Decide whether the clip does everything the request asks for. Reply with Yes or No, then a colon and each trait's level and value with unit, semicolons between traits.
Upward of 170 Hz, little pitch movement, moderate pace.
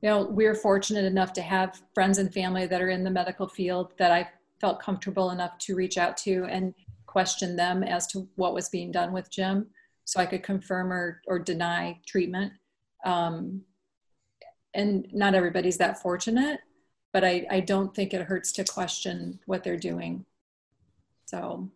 Yes: medium, 185 Hz; narrow, 1.4 semitones; average, 175 wpm